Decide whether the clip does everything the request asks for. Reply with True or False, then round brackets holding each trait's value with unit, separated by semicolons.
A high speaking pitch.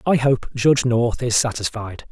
False (120 Hz)